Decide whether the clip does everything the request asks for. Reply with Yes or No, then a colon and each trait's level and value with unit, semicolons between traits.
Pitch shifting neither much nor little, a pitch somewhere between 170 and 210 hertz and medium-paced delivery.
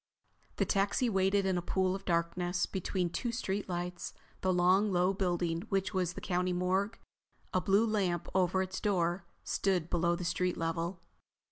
No: narrow, 1.8 semitones; medium, 185 Hz; average, 165 wpm